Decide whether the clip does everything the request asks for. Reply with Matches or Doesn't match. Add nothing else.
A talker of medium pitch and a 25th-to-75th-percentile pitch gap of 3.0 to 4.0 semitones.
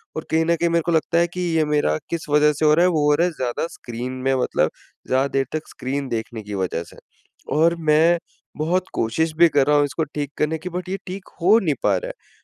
Matches